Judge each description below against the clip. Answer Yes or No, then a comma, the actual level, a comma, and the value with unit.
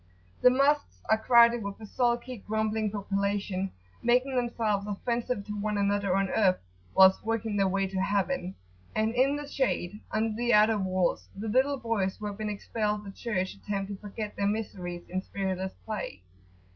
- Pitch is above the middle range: Yes, high, 210 Hz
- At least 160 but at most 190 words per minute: Yes, average, 170 wpm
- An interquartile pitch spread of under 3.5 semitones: Yes, average, 2.9 semitones